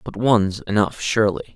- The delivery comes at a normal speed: Yes, average, 155 wpm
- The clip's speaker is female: No, male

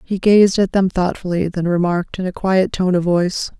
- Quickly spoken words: Yes, fast, 215 wpm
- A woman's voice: Yes, female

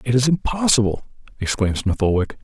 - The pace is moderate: Yes, average, 150 wpm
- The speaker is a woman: No, male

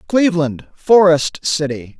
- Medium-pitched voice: Yes, medium, 165 Hz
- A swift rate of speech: No, slow, 90 wpm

